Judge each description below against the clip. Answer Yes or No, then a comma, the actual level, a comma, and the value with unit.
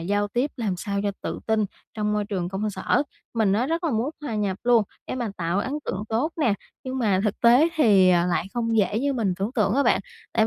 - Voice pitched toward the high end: Yes, high, 215 Hz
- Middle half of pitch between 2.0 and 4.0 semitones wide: Yes, average, 3.5 semitones